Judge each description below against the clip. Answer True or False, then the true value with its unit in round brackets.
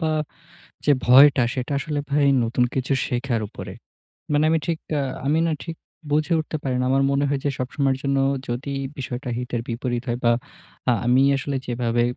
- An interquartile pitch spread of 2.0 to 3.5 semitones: True (2.9 semitones)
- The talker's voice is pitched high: False (135 Hz)